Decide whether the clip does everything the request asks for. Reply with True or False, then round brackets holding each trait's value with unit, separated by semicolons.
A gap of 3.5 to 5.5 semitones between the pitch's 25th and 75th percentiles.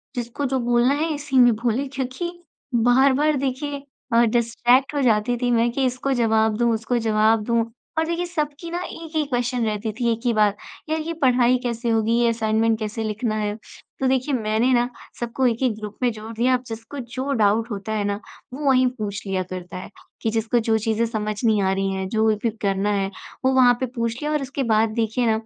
False (3.1 semitones)